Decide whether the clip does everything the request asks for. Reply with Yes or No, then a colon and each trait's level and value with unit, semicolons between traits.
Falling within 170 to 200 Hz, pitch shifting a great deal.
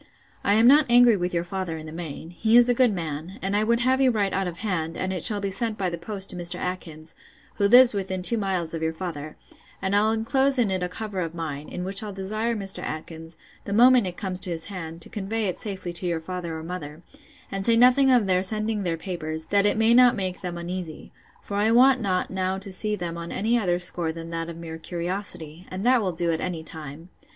No: medium, 185 Hz; average, 4.2 semitones